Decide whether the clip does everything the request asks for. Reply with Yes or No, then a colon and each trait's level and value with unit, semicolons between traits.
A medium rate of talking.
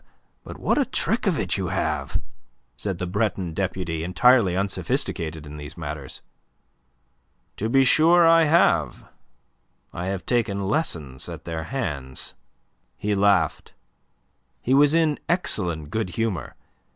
No: slow, 130 wpm